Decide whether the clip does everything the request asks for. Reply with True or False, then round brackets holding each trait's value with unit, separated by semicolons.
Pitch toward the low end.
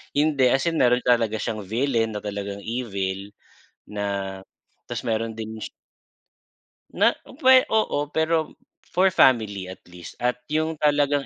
True (115 Hz)